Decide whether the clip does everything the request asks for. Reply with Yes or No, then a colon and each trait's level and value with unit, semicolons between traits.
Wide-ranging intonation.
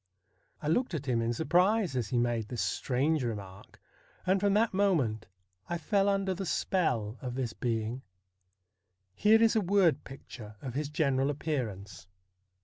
Yes: wide, 8.1 semitones